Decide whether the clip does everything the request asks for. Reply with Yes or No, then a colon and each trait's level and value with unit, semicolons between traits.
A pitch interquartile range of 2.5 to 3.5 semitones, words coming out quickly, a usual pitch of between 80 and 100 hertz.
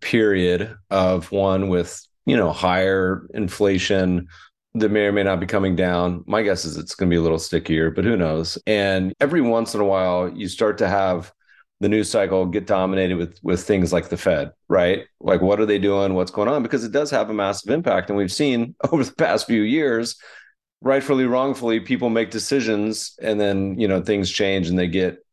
Yes: average, 3.1 semitones; fast, 210 wpm; very low, 95 Hz